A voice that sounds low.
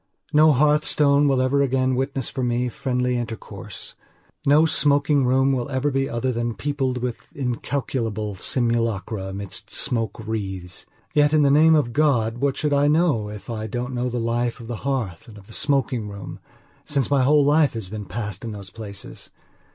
Yes: low, 125 Hz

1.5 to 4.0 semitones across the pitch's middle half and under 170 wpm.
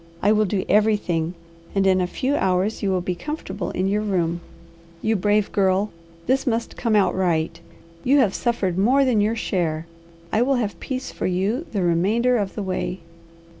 No: average, 3.7 semitones; average, 185 wpm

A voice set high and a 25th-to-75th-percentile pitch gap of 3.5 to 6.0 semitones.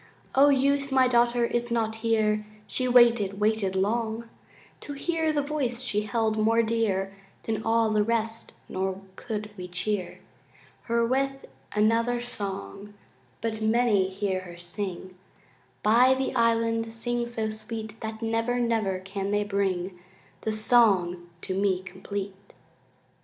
No: high, 220 Hz; average, 3.0 semitones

